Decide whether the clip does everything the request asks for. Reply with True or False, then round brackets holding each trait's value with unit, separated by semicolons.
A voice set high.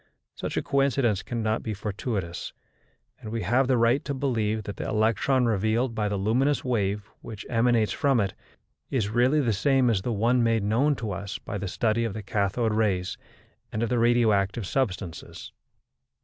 False (110 Hz)